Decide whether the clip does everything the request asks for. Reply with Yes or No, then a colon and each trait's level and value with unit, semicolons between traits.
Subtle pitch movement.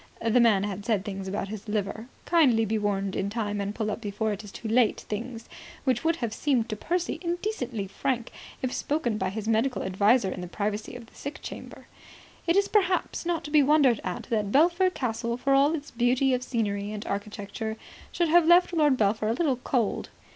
No: average, 5.3 semitones